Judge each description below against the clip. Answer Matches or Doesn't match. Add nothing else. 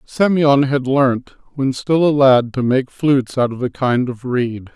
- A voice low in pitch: Matches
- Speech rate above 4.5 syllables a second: Doesn't match